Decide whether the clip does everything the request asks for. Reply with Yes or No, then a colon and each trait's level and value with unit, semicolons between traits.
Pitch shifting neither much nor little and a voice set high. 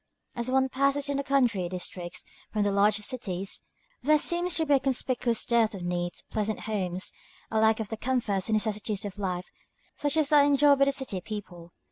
No: wide, 5.7 semitones; high, 220 Hz